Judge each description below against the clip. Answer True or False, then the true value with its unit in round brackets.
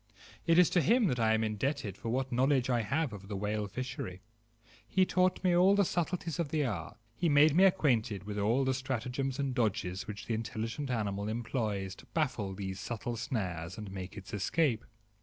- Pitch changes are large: True (5.8 semitones)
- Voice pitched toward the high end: False (120 Hz)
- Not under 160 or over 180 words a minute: False (195 wpm)